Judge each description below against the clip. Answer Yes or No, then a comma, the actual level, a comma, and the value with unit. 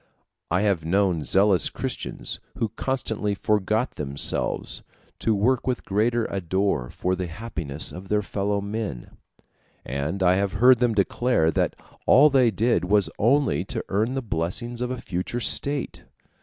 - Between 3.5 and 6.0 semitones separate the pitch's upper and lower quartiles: Yes, average, 4.5 semitones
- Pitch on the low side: Yes, low, 100 Hz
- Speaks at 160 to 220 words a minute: No, average, 150 wpm